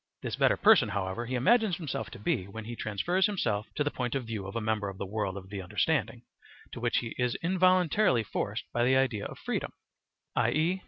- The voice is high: No, low, 120 Hz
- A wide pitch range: Yes, wide, 7.9 semitones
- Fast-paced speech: Yes, fast, 215 wpm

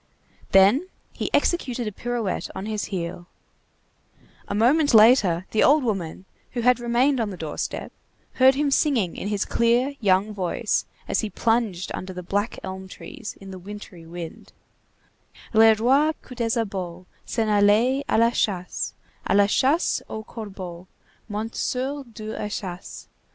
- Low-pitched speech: No, high, 215 Hz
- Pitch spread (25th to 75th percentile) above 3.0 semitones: Yes, average, 4.3 semitones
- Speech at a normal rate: Yes, average, 150 wpm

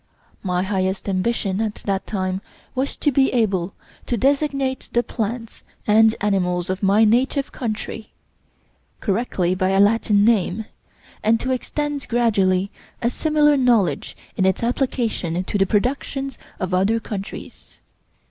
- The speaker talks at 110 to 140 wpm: Yes, slow, 135 wpm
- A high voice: Yes, high, 215 Hz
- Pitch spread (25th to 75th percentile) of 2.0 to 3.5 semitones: No, average, 4.5 semitones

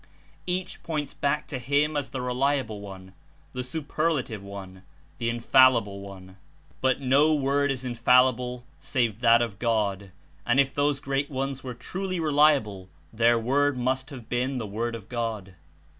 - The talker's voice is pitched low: Yes, low, 125 Hz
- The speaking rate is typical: Yes, average, 160 wpm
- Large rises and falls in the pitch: No, average, 3.9 semitones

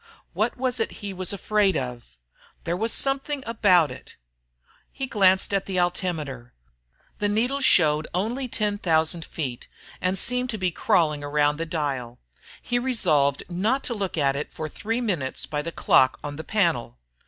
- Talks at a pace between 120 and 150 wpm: No, average, 165 wpm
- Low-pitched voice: No, medium, 180 Hz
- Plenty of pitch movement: Yes, wide, 6.6 semitones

